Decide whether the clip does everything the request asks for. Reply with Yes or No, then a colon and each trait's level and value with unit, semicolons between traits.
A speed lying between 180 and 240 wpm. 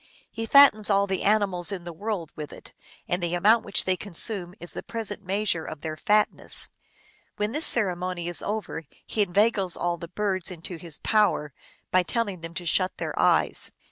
Yes: average, 190 wpm